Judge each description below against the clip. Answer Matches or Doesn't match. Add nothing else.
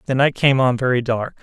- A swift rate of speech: Matches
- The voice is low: Matches